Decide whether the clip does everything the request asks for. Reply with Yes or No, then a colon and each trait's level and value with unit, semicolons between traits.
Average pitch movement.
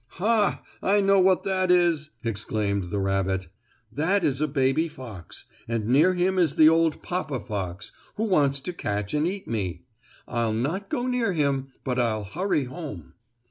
No: wide, 8.6 semitones